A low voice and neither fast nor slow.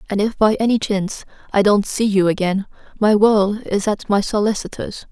No: high, 205 Hz; average, 190 wpm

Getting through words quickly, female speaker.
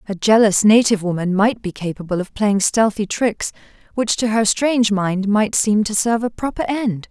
No: average, 195 wpm; female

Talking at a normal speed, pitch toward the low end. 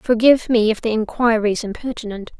No: average, 175 wpm; high, 225 Hz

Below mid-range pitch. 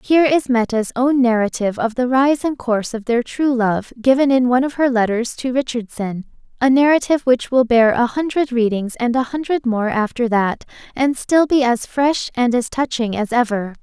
No: high, 245 Hz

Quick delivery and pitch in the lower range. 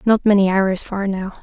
No: fast, 210 wpm; high, 195 Hz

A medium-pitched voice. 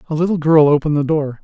Yes: medium, 155 Hz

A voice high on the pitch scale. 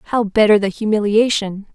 Yes: high, 210 Hz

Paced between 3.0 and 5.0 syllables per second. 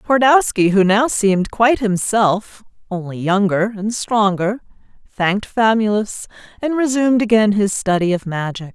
Yes: 4.6 syllables/s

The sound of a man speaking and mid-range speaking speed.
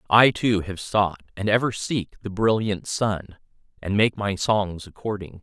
Yes: male; average, 165 wpm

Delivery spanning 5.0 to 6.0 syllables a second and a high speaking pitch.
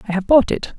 No: 6.6 syllables/s; high, 220 Hz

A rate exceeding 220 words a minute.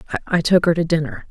Yes: fast, 230 wpm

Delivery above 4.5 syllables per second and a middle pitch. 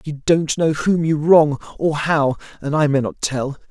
No: 4.2 syllables/s; medium, 150 Hz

